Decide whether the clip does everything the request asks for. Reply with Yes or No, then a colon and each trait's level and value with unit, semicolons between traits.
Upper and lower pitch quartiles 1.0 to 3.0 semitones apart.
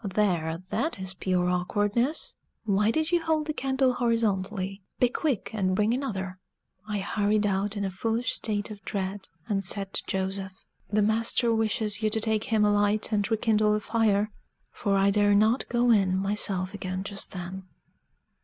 Yes: narrow, 2.5 semitones